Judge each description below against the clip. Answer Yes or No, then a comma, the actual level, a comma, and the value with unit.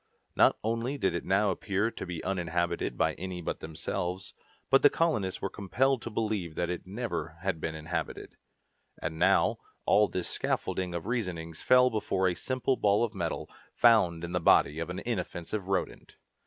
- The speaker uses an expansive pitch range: No, average, 4.5 semitones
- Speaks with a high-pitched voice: No, very low, 95 Hz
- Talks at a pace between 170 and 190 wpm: Yes, average, 175 wpm